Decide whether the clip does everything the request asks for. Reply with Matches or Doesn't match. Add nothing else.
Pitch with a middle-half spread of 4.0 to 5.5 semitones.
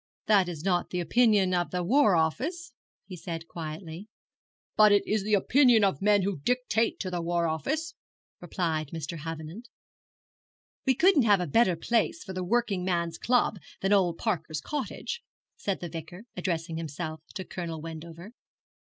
Matches